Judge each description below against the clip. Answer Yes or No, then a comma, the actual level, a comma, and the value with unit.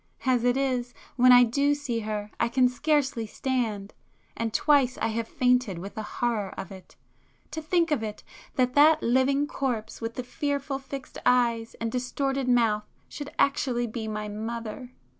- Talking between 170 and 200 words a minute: No, average, 160 wpm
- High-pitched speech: Yes, high, 245 Hz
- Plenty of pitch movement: No, average, 3.3 semitones